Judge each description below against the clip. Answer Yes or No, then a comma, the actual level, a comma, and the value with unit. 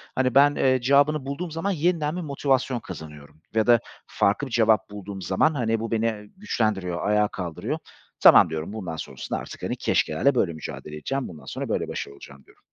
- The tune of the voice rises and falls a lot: Yes, wide, 7.3 semitones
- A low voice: Yes, low, 115 Hz